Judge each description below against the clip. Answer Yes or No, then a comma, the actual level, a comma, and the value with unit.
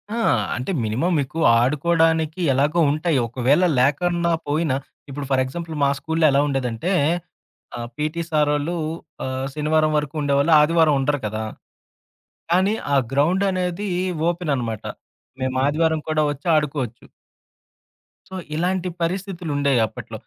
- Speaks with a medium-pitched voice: Yes, medium, 150 Hz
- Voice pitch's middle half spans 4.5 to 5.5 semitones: No, average, 3.7 semitones